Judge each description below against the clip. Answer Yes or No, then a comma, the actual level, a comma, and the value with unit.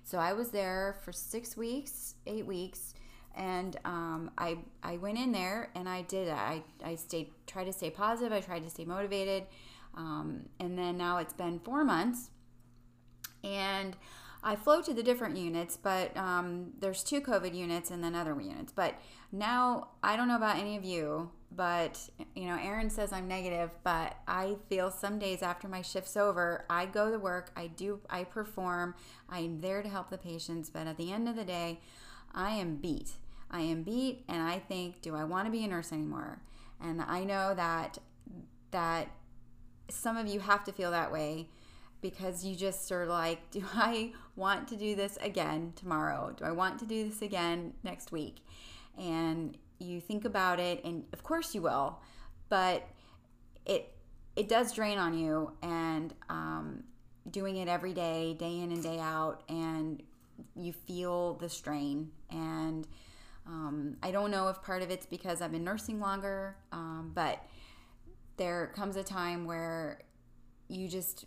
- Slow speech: No, average, 175 wpm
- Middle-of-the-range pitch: Yes, medium, 180 Hz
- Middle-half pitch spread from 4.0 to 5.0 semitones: No, average, 3.3 semitones